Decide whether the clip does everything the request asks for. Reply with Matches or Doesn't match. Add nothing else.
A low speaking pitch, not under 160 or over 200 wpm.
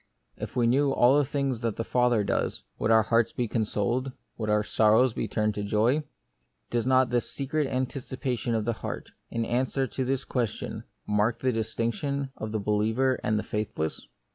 Matches